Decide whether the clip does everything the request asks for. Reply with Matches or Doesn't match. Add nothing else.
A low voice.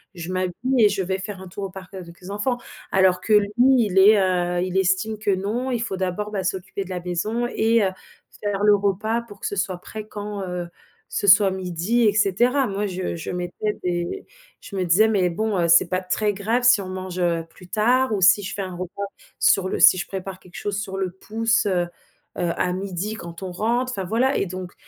Doesn't match